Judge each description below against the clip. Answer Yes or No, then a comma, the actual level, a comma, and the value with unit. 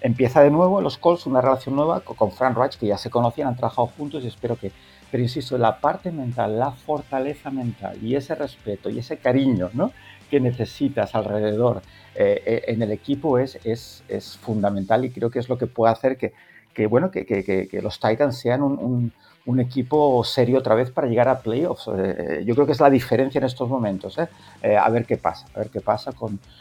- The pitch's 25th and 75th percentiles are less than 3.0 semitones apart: No, average, 3.8 semitones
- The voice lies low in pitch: Yes, low, 125 Hz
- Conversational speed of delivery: No, fast, 210 wpm